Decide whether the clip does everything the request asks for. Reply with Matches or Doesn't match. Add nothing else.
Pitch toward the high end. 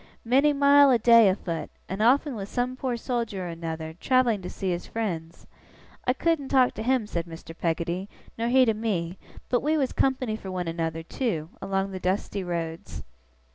Matches